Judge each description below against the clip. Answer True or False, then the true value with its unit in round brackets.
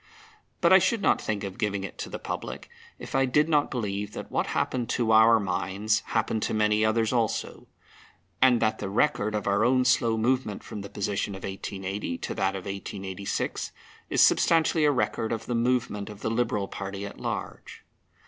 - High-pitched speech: False (110 Hz)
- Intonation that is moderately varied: True (3.5 semitones)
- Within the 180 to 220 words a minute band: True (190 wpm)